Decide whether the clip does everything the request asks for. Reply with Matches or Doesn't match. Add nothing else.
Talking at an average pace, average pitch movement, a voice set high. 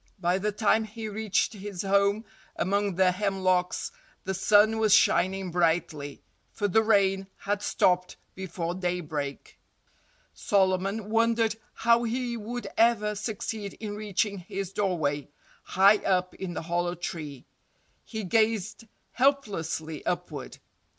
Doesn't match